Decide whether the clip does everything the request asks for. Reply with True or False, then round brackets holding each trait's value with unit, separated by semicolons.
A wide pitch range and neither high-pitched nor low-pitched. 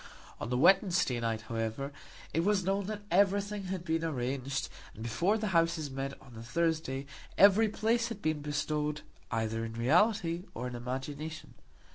True (7.2 semitones; 155 Hz)